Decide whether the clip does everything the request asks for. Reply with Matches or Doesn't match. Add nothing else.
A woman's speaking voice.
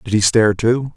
Doesn't match